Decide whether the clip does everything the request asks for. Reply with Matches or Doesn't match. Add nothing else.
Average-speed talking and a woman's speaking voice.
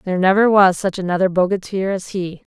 Matches